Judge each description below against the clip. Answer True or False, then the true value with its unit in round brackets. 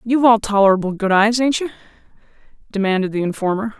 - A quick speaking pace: False (160 wpm)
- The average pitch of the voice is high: True (215 Hz)